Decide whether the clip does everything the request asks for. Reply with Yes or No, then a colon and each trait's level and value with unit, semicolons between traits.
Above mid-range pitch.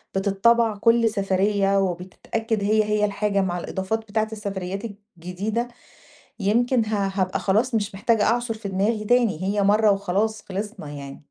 Yes: high, 205 Hz